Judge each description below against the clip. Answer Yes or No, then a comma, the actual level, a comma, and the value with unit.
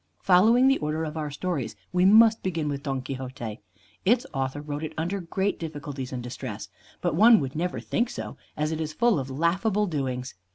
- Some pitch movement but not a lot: No, wide, 5.8 semitones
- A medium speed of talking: Yes, average, 195 wpm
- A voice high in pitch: No, medium, 155 Hz